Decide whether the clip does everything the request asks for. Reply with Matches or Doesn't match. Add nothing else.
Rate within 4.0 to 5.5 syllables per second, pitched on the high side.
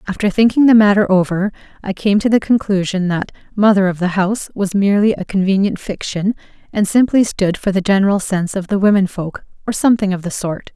Doesn't match